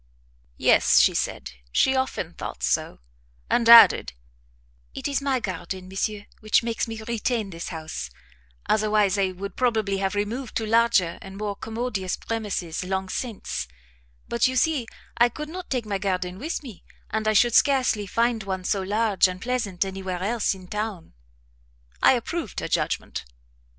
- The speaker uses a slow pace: No, average, 160 wpm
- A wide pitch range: No, average, 3.6 semitones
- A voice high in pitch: Yes, high, 210 Hz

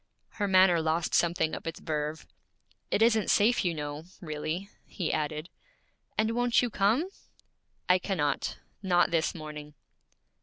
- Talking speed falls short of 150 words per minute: Yes, average, 140 wpm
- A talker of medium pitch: Yes, medium, 175 Hz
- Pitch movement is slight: No, average, 4.7 semitones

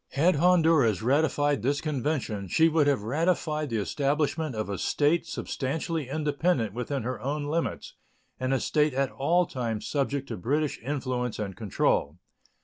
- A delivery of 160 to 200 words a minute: No, average, 150 wpm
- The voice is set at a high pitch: No, medium, 140 Hz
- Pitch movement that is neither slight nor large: Yes, average, 3.9 semitones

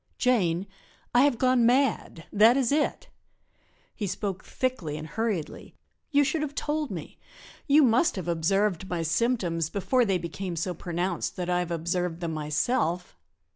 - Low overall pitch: No, high, 190 Hz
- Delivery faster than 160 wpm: No, average, 155 wpm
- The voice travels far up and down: Yes, wide, 6.7 semitones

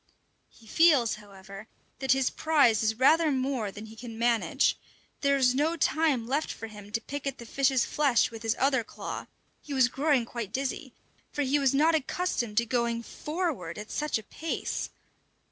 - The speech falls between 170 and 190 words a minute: Yes, average, 180 wpm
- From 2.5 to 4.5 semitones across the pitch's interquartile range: Yes, average, 4.2 semitones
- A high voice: Yes, very high, 255 Hz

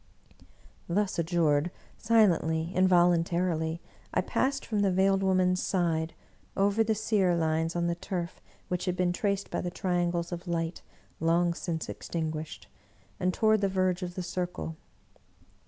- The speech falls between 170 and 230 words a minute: No, average, 150 wpm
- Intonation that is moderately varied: No, narrow, 2.2 semitones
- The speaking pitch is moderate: Yes, medium, 175 Hz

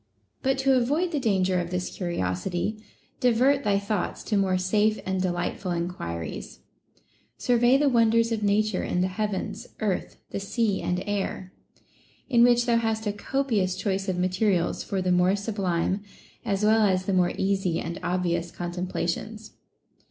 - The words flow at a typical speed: Yes, average, 160 wpm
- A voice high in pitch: Yes, high, 200 Hz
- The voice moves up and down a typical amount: Yes, average, 3.6 semitones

